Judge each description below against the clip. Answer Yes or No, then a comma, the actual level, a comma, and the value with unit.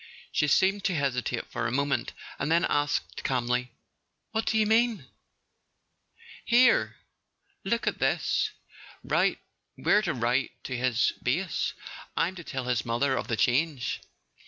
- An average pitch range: No, wide, 8.0 semitones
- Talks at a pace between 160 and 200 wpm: No, average, 140 wpm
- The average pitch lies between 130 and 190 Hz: Yes, medium, 140 Hz